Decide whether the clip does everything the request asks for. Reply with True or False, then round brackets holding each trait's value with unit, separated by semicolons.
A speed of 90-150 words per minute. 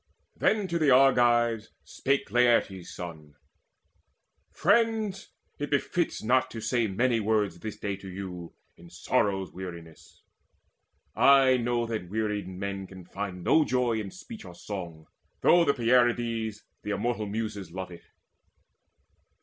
True (135 wpm)